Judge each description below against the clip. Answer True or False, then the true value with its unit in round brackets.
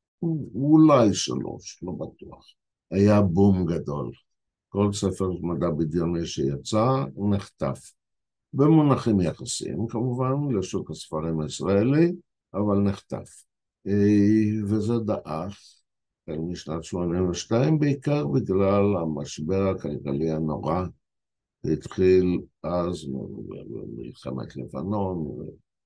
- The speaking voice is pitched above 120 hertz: False (100 Hz)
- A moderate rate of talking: False (85 wpm)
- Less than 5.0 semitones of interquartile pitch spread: True (4.3 semitones)